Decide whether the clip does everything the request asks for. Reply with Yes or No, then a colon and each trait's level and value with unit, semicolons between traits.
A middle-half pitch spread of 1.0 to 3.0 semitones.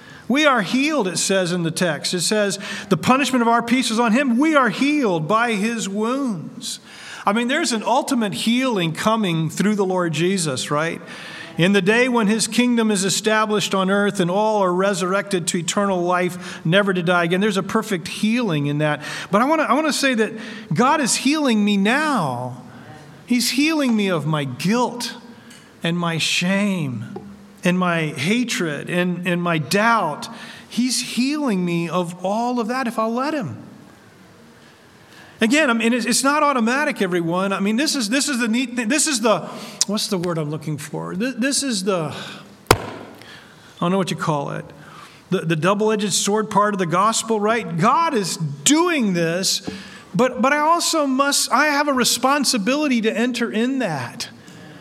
No: average, 5.1 semitones